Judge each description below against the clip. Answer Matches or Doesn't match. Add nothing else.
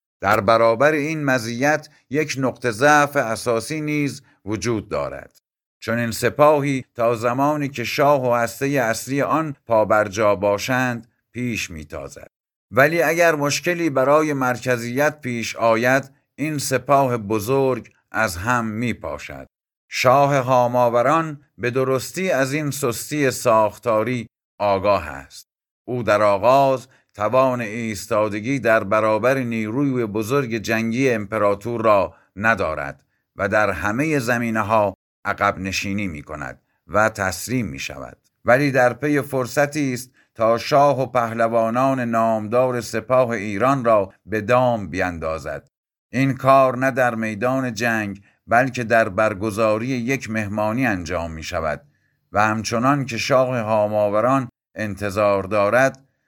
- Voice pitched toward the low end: Matches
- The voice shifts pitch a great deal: Doesn't match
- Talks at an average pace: Matches